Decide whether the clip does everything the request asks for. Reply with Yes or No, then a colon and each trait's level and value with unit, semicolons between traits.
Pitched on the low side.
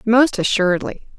No: high, 215 Hz